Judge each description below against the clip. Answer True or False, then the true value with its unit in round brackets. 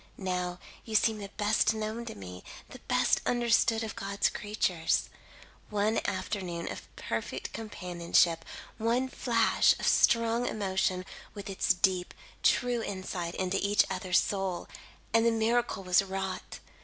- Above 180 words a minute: False (135 wpm)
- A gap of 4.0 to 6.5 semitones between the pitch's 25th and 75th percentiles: False (3.4 semitones)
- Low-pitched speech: False (200 Hz)